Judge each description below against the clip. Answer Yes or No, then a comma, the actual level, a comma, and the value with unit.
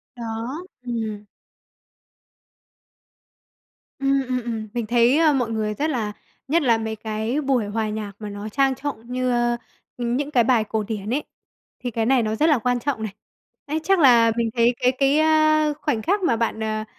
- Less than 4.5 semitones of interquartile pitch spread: Yes, average, 3.9 semitones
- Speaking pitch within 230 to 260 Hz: Yes, high, 240 Hz